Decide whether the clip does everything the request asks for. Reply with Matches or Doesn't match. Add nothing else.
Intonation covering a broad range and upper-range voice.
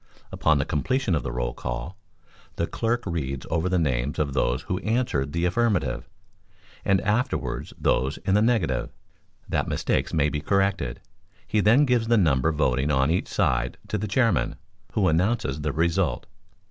Doesn't match